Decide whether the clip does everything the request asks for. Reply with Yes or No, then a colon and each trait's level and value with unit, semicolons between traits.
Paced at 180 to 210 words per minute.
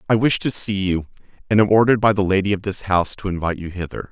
No: fast, 265 wpm